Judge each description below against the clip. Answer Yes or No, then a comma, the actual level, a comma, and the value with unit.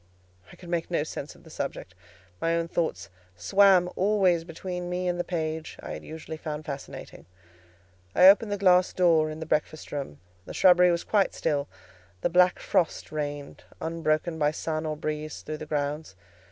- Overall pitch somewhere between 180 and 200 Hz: No, medium, 160 Hz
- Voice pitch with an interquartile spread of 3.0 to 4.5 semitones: No, narrow, 2.6 semitones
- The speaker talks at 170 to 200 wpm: Yes, average, 180 wpm